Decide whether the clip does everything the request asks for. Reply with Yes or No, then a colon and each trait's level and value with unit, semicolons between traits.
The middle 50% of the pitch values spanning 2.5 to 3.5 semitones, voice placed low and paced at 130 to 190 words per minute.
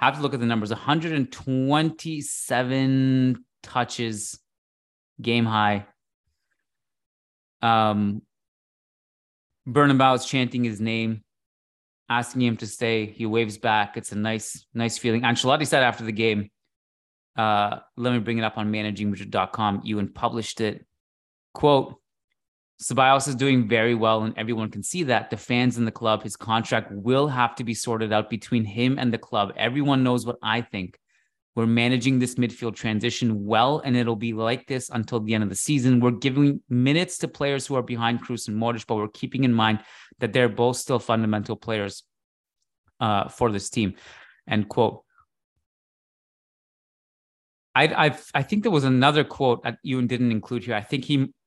Yes: average, 2.9 semitones; low, 115 Hz; average, 165 wpm